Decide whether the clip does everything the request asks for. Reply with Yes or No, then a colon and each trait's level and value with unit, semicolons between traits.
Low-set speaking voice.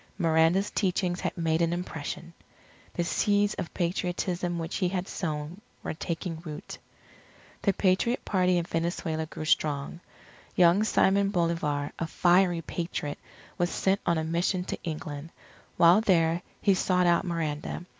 No: medium, 175 Hz